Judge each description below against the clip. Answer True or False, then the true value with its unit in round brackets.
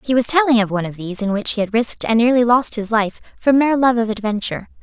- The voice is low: False (230 Hz)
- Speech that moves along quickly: True (275 wpm)